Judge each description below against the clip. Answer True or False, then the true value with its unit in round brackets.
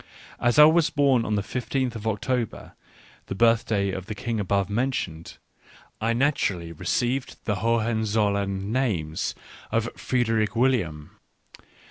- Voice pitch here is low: True (110 Hz)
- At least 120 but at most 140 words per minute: True (135 wpm)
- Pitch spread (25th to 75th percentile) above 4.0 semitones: False (3.7 semitones)